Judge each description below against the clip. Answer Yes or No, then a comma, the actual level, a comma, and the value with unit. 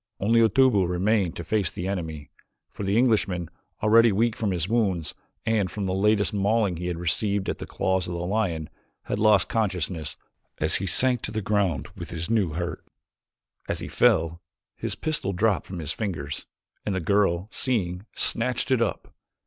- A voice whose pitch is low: Yes, low, 100 Hz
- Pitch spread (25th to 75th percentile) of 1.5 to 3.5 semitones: No, average, 3.9 semitones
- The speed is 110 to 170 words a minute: No, average, 180 wpm